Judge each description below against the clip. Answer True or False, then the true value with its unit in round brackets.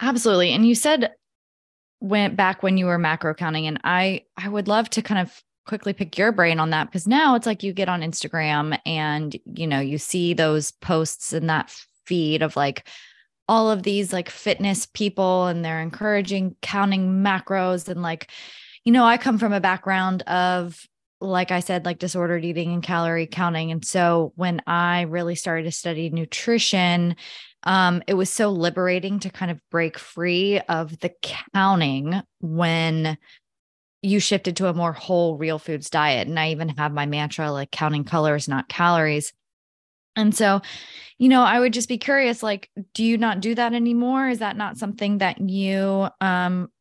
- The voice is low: False (180 Hz)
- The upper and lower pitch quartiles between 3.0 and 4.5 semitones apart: True (3.7 semitones)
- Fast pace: False (180 wpm)